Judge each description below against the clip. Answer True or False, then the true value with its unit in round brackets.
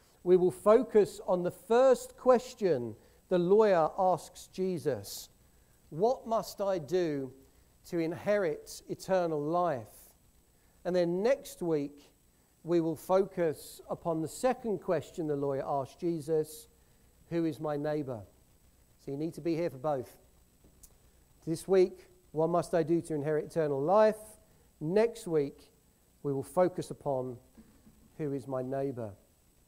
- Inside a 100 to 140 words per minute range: True (135 wpm)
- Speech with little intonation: False (5.0 semitones)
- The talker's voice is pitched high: False (165 Hz)